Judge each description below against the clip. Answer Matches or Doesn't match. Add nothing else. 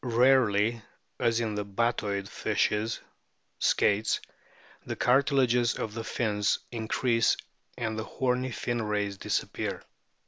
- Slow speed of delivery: Matches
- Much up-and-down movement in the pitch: Doesn't match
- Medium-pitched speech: Doesn't match